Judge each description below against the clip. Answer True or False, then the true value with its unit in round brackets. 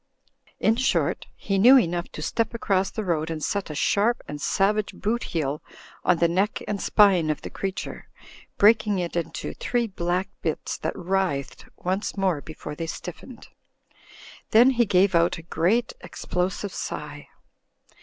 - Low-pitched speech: False (185 Hz)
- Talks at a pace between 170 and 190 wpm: False (155 wpm)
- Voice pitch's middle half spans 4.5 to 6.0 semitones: False (4.1 semitones)